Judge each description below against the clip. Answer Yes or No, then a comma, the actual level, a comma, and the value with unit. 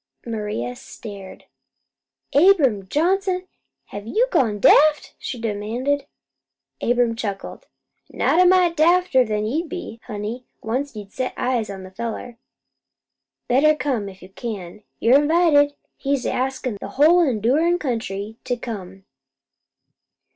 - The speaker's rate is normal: No, slow, 120 wpm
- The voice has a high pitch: Yes, high, 245 Hz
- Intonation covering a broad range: Yes, wide, 6.1 semitones